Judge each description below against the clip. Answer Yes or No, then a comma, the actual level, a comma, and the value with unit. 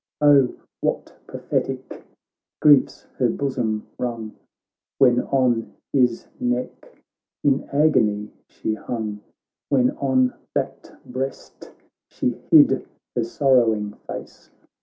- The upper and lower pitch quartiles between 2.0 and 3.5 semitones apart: Yes, average, 3.1 semitones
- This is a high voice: No, low, 125 Hz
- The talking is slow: Yes, slow, 100 wpm